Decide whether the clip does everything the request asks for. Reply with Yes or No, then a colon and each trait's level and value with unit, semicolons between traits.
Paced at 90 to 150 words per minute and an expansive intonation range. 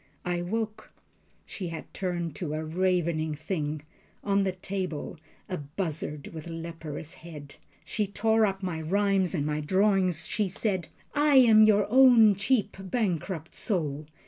No: average, 145 wpm; average, 4.2 semitones